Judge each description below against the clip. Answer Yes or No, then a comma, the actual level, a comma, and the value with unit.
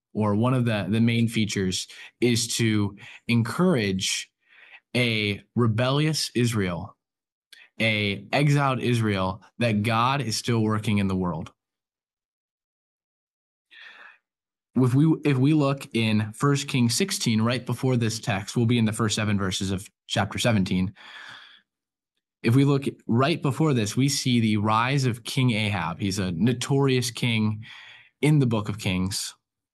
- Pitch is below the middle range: Yes, low, 115 Hz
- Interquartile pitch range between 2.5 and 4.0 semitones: Yes, average, 3.7 semitones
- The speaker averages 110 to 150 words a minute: Yes, average, 140 wpm